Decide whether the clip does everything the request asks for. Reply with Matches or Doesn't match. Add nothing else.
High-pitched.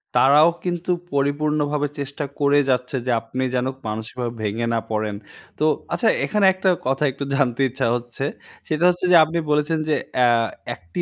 Doesn't match